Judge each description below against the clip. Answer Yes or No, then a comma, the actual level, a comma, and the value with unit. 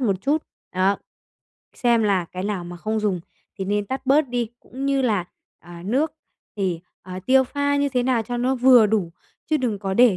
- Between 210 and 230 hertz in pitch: Yes, high, 225 Hz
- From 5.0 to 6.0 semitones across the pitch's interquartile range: Yes, average, 5.3 semitones